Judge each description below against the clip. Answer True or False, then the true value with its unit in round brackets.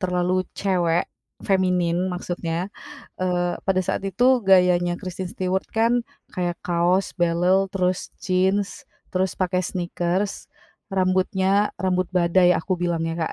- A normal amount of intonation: False (1.3 semitones)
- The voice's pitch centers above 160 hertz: True (185 Hz)